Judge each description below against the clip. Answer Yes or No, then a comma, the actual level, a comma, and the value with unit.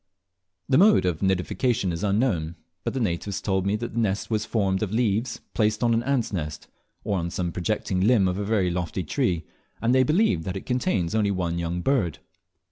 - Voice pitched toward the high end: No, low, 100 Hz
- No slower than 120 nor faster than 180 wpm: No, fast, 205 wpm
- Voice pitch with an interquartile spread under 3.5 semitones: No, average, 4.5 semitones